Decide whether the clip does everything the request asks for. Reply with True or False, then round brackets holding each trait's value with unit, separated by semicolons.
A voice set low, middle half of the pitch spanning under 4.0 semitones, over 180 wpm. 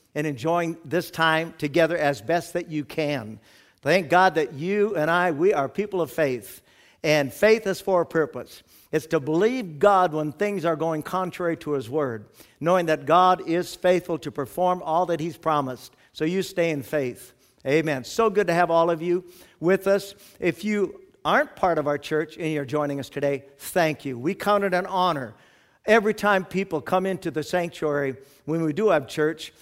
False (165 Hz; 3.6 semitones; 195 wpm)